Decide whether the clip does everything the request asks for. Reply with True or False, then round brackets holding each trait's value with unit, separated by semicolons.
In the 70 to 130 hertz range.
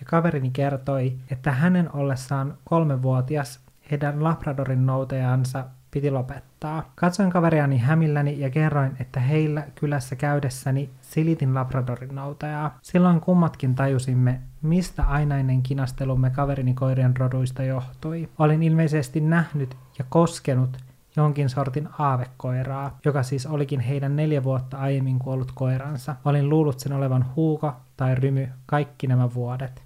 False (140 Hz)